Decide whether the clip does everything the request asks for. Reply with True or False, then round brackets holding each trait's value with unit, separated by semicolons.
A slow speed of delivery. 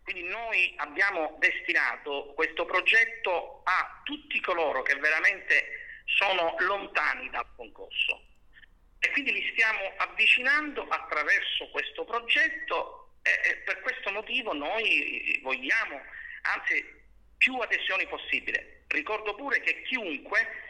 True (105 wpm)